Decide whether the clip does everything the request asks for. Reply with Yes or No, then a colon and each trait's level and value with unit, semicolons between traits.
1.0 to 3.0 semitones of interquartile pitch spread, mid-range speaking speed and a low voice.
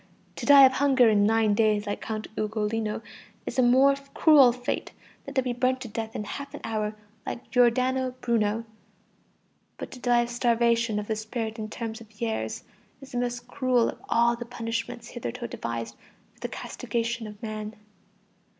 No: narrow, 2.4 semitones; average, 180 wpm; high, 235 Hz